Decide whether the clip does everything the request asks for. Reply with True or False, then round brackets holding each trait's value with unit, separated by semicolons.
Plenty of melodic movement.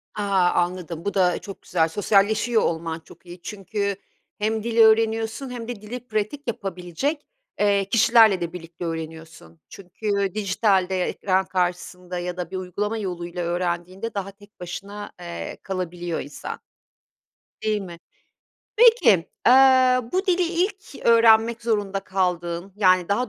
False (4.0 semitones)